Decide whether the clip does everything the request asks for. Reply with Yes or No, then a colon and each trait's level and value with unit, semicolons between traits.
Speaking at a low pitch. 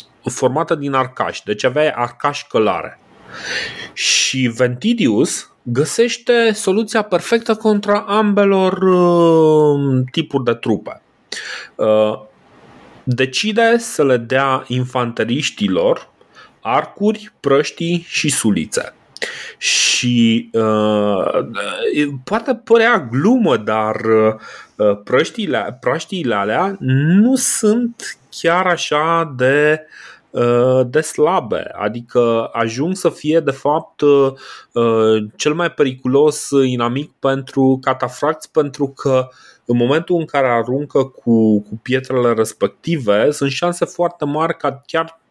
No: medium, 145 Hz